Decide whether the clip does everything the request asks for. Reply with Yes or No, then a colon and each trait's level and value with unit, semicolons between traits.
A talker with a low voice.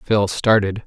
Yes: low, 105 Hz